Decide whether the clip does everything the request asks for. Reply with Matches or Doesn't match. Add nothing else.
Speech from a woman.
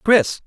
Doesn't match